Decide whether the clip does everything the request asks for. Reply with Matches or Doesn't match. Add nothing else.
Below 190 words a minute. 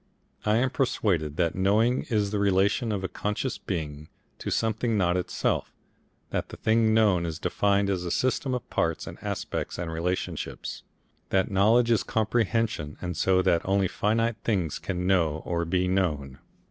Matches